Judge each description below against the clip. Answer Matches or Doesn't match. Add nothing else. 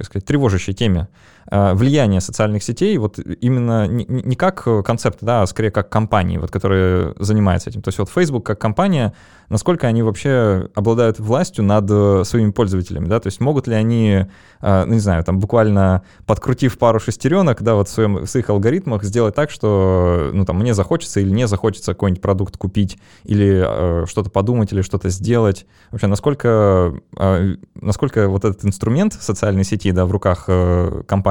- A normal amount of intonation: Matches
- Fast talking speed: Matches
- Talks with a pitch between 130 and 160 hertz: Doesn't match